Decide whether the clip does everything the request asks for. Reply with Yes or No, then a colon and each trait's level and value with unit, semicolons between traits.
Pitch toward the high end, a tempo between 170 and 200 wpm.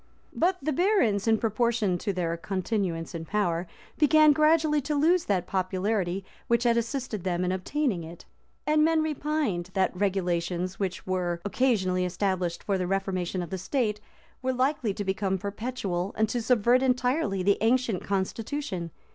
No: high, 205 Hz; average, 155 wpm